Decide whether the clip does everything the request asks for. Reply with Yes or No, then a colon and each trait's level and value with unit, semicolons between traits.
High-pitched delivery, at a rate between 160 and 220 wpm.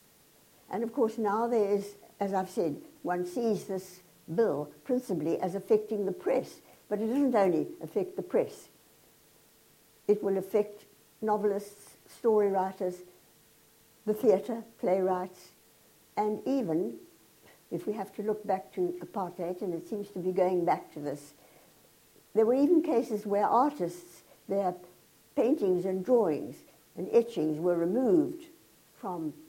No: high, 200 Hz; average, 140 wpm